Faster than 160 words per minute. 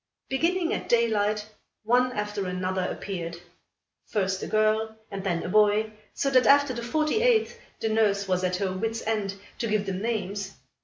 Yes: average, 170 wpm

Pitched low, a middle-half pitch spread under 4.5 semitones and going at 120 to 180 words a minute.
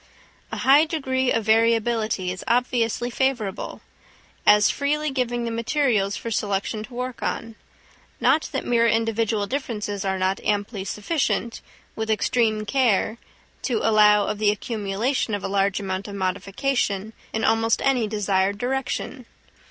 No: high, 225 Hz; average, 3.4 semitones; average, 140 wpm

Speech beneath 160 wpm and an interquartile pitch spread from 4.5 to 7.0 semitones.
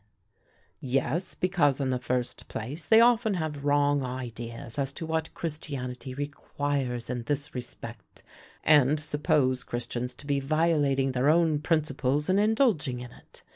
No: average, 140 wpm; average, 3.6 semitones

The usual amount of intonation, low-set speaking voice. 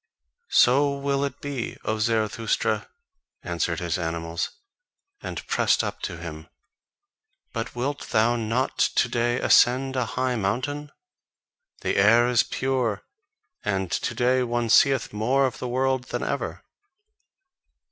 Yes: average, 3.3 semitones; low, 120 Hz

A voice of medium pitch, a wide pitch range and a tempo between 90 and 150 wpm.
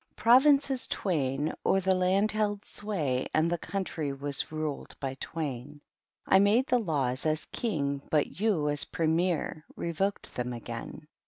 Yes: medium, 160 Hz; wide, 5.9 semitones; average, 145 wpm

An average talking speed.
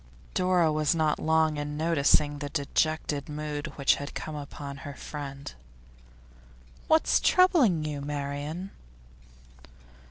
No: slow, 115 wpm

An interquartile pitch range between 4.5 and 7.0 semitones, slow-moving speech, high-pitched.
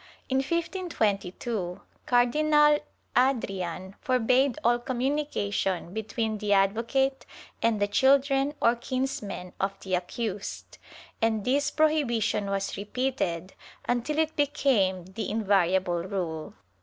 Yes: wide, 5.5 semitones; slow, 105 wpm; high, 225 Hz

